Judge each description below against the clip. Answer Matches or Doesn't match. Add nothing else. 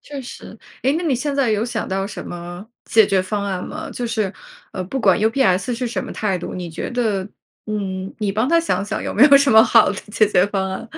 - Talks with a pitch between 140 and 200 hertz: Doesn't match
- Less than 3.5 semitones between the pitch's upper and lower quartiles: Doesn't match